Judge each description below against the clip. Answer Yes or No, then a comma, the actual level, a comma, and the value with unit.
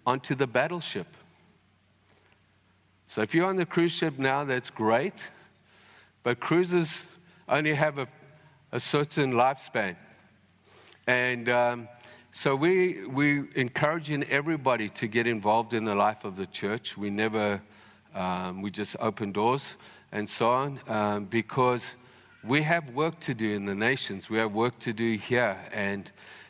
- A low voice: Yes, low, 120 Hz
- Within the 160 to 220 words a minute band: No, average, 145 wpm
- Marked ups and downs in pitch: Yes, wide, 5.7 semitones